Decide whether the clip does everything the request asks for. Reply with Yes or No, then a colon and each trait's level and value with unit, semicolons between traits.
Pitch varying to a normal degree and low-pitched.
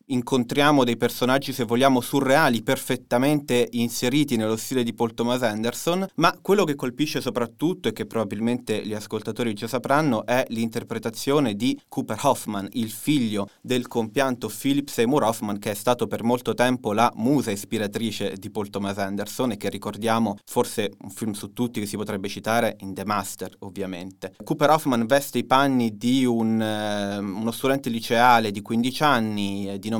Yes: average, 3.6 semitones; low, 120 Hz